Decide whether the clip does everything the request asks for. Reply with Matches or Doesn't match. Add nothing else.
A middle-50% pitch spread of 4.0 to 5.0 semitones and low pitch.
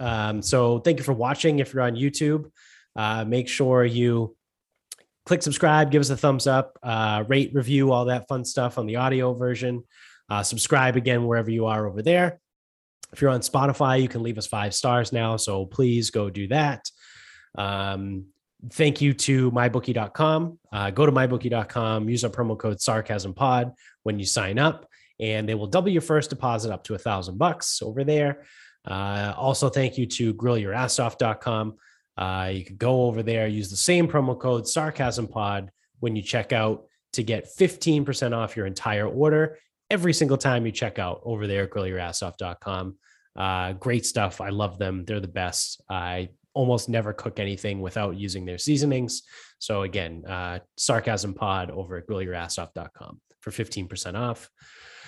Matches